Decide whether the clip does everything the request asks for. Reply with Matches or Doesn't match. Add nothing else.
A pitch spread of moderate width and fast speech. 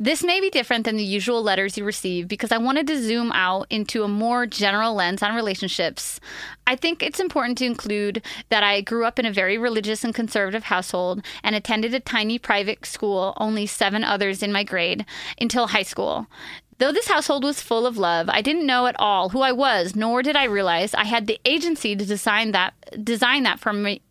Matches